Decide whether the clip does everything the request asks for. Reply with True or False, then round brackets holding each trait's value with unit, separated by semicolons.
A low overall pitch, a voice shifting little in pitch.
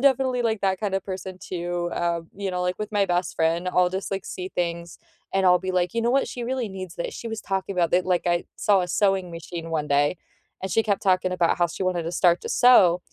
False (185 Hz; 2.3 semitones)